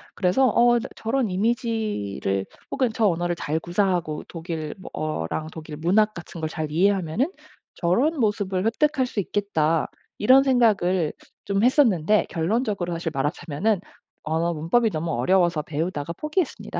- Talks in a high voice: No, medium, 180 Hz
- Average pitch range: No, wide, 5.8 semitones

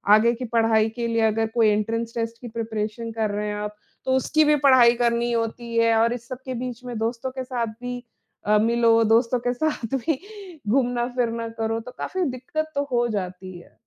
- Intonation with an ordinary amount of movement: No, narrow, 1.7 semitones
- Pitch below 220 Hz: No, high, 235 Hz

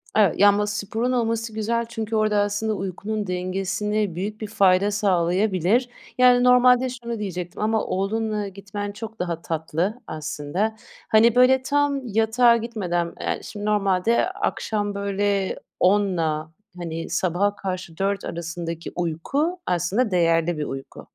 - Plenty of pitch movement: No, average, 3.8 semitones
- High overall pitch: Yes, high, 205 Hz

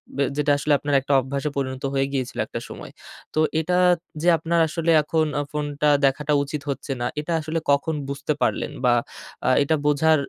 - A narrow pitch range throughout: Yes, narrow, 2.2 semitones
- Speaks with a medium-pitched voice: Yes, medium, 145 Hz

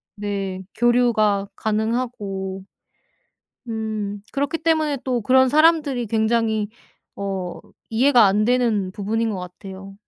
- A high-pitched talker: Yes, high, 220 Hz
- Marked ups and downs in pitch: No, average, 3.8 semitones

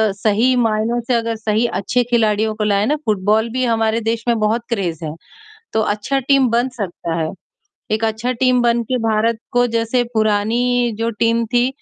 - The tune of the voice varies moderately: No, narrow, 2.1 semitones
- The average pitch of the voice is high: Yes, high, 225 Hz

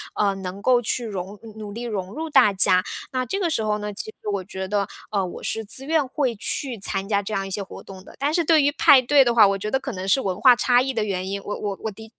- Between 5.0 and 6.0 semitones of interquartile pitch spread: No, average, 4.6 semitones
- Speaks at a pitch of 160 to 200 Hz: No, high, 215 Hz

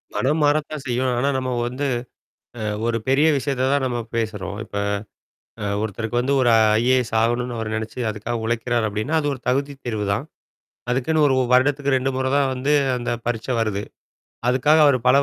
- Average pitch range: Yes, average, 3.2 semitones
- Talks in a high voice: No, low, 125 Hz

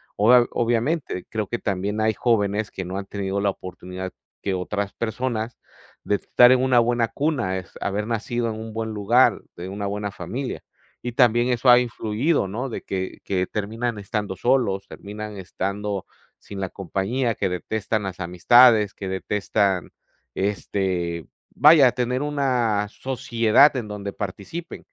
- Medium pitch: No, low, 105 Hz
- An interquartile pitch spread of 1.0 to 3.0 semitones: No, average, 3.6 semitones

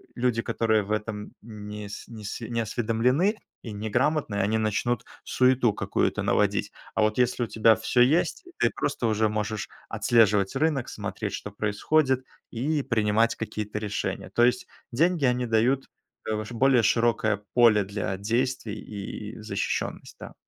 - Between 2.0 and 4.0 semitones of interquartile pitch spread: Yes, average, 2.9 semitones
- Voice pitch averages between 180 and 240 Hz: No, low, 115 Hz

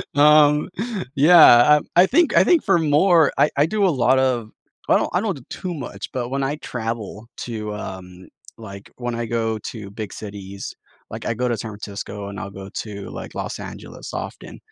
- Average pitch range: No, wide, 6.1 semitones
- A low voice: Yes, low, 120 Hz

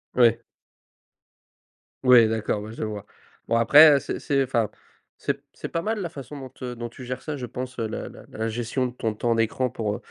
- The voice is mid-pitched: No, low, 120 Hz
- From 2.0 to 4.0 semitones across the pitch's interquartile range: Yes, average, 2.9 semitones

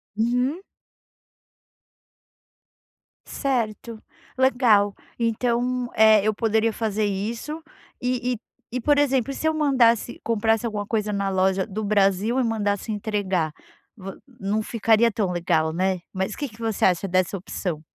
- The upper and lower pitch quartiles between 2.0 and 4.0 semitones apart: Yes, average, 3.4 semitones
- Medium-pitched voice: No, high, 220 Hz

